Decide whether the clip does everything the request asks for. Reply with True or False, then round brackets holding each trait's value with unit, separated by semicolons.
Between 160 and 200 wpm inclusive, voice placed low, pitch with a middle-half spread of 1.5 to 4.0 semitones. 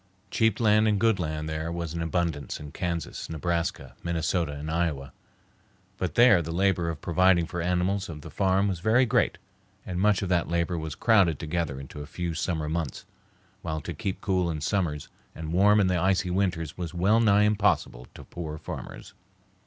True (185 wpm; 85 Hz; 3.3 semitones)